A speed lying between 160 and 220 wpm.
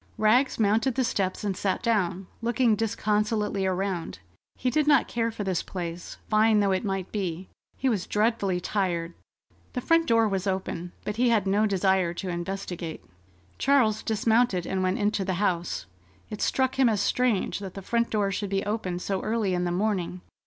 Yes: average, 180 wpm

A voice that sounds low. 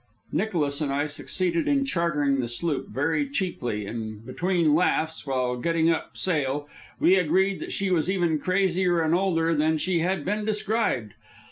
No: medium, 165 Hz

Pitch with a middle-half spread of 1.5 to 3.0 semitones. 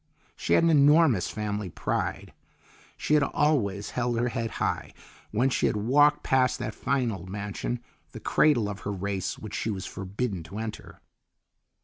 No: average, 4.7 semitones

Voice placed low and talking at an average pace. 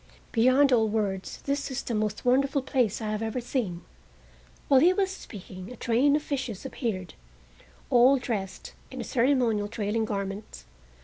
No: high, 235 Hz; average, 150 wpm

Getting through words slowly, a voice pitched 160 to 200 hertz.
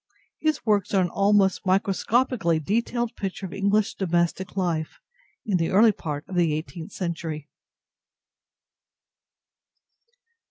Yes: slow, 115 wpm; high, 190 Hz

